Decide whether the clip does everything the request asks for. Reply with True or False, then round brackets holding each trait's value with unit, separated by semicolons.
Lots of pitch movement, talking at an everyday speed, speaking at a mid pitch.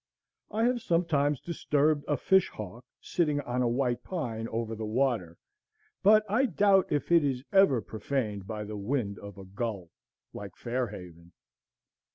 False (7.5 semitones; 155 wpm; 125 Hz)